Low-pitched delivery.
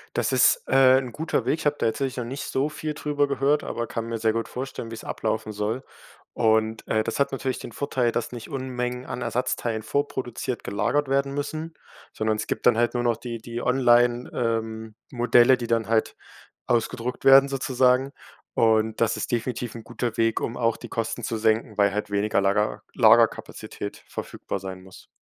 Yes: low, 120 Hz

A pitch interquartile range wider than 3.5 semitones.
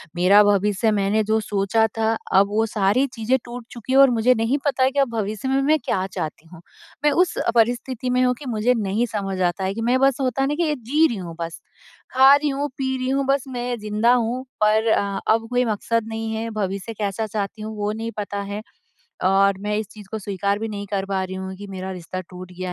Yes: average, 4.0 semitones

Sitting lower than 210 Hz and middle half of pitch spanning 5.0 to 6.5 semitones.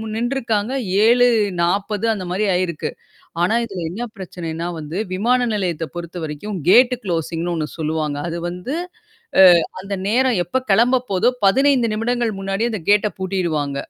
Yes: high, 195 Hz; average, 5.3 semitones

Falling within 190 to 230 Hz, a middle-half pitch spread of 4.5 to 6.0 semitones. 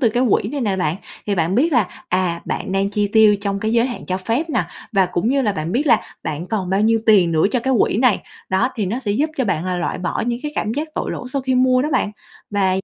Yes: high, 210 Hz; average, 5.1 semitones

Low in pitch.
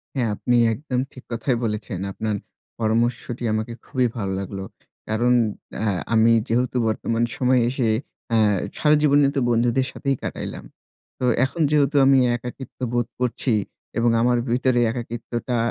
Yes: low, 120 Hz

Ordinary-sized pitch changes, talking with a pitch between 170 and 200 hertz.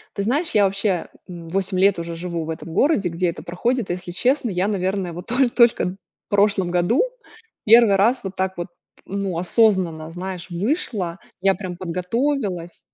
Yes: average, 3.3 semitones; high, 190 Hz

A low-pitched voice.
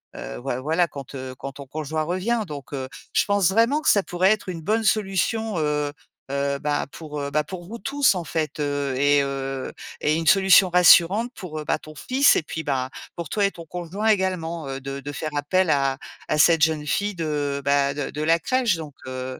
No: medium, 155 Hz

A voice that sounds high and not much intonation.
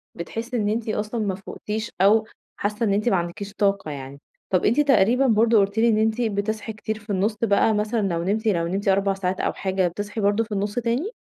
Yes: high, 210 Hz; narrow, 2.3 semitones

